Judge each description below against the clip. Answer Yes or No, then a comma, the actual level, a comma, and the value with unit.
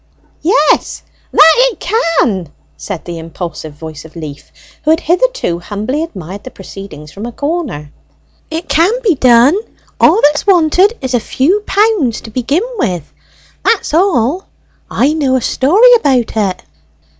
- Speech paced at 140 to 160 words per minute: Yes, average, 145 wpm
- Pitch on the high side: Yes, very high, 265 Hz